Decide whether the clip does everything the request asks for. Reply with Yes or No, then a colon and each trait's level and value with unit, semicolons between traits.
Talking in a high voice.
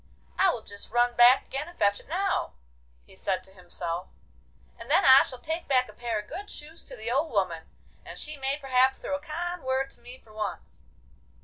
Yes: very high, 260 Hz